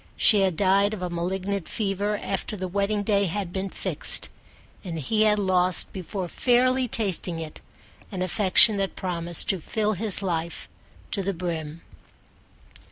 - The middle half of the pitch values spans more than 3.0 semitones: No, narrow, 2.5 semitones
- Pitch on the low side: No, high, 195 Hz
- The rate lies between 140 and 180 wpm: Yes, average, 155 wpm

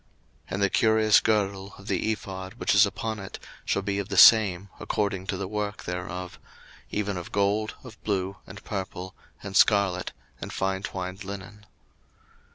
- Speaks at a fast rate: No, average, 165 wpm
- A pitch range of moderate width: No, narrow, 1.7 semitones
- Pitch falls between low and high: No, low, 100 Hz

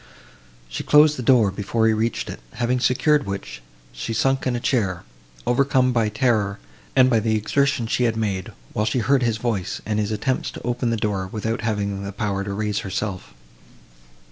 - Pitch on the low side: Yes, low, 110 Hz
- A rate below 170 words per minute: No, average, 190 wpm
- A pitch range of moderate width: Yes, average, 3.4 semitones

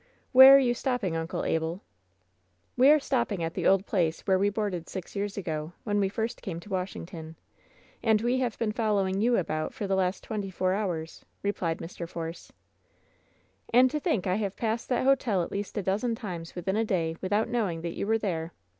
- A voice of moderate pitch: No, high, 195 Hz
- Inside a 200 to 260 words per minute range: Yes, fast, 205 wpm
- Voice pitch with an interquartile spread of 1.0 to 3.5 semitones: No, average, 4.8 semitones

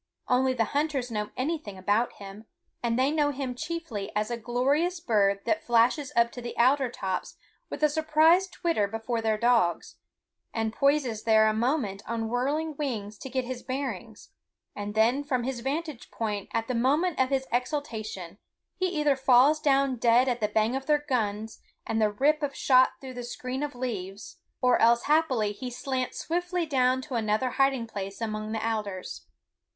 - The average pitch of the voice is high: Yes, high, 245 Hz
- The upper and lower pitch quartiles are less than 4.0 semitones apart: No, average, 4.3 semitones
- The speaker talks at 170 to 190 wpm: Yes, average, 180 wpm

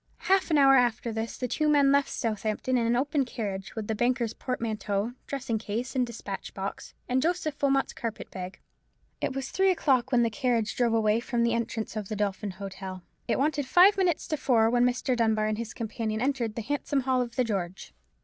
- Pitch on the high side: Yes, high, 235 Hz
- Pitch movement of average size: Yes, average, 3.8 semitones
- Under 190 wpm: No, fast, 205 wpm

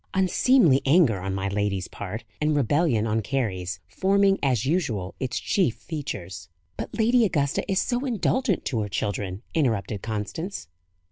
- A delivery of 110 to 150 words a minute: Yes, average, 145 wpm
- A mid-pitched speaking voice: No, low, 130 Hz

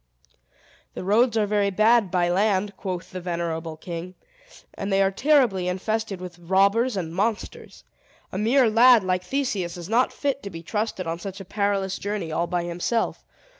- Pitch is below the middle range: No, high, 195 Hz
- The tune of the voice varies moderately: Yes, average, 3.5 semitones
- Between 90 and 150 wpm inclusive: No, average, 170 wpm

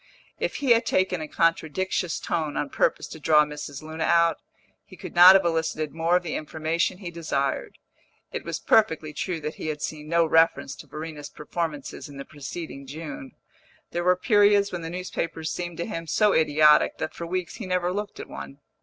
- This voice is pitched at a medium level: Yes, medium, 165 Hz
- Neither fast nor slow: Yes, average, 195 wpm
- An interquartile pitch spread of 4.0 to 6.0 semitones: No, average, 2.7 semitones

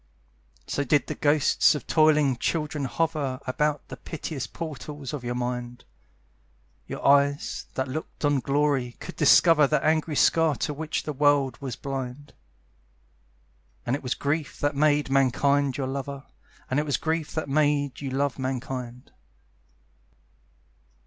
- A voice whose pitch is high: No, medium, 140 Hz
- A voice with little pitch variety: Yes, narrow, 2.3 semitones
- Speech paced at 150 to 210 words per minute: No, average, 140 wpm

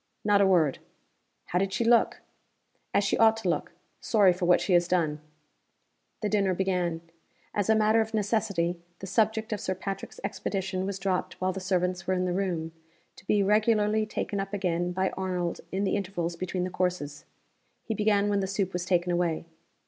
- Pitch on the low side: No, high, 190 Hz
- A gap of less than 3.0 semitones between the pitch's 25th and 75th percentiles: Yes, narrow, 2.4 semitones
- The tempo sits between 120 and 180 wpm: No, average, 190 wpm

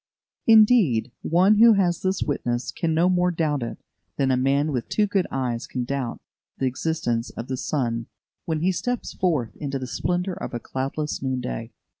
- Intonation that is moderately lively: No, wide, 6.0 semitones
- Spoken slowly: No, average, 185 wpm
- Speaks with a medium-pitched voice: Yes, medium, 145 Hz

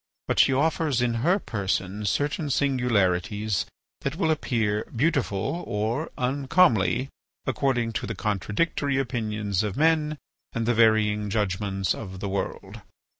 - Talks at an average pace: No, slow, 125 wpm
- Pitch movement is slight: No, average, 5.1 semitones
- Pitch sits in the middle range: No, low, 115 Hz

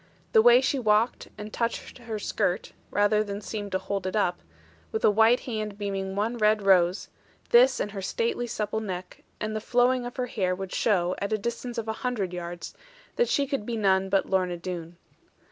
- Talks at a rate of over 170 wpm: Yes, average, 200 wpm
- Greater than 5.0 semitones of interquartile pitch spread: No, average, 3.6 semitones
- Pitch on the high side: Yes, high, 210 Hz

